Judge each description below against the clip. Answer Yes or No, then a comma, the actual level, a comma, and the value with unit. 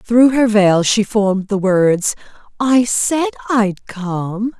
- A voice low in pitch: No, high, 215 Hz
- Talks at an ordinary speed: Yes, average, 145 wpm